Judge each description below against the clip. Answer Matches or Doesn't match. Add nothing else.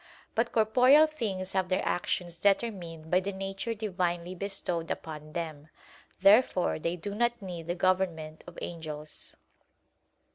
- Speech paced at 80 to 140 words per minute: Matches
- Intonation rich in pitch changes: Doesn't match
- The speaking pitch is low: Doesn't match